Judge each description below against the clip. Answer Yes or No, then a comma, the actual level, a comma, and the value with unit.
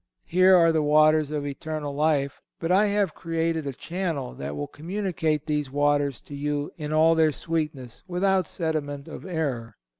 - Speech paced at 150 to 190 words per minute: Yes, average, 170 wpm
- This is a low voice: No, medium, 155 Hz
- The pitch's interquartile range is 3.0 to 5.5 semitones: No, narrow, 2.5 semitones